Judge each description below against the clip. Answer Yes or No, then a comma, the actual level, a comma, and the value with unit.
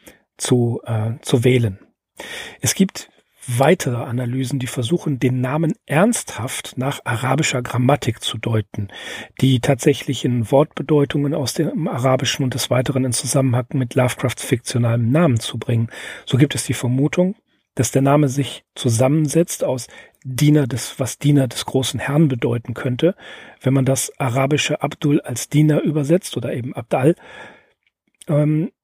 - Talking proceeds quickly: No, average, 140 wpm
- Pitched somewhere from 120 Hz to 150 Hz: Yes, low, 135 Hz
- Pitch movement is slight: No, average, 3.1 semitones